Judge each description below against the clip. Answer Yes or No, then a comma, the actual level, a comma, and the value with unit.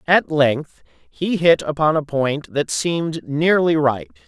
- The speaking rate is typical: Yes, average, 155 wpm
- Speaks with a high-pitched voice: No, medium, 150 Hz